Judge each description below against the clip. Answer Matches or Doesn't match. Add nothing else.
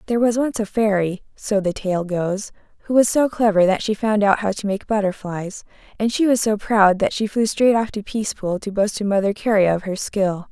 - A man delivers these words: Doesn't match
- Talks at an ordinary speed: Doesn't match